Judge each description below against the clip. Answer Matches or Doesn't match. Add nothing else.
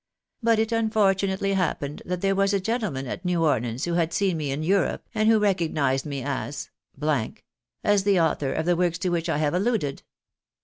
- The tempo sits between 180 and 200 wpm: Matches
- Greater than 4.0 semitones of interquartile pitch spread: Matches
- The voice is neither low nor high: Matches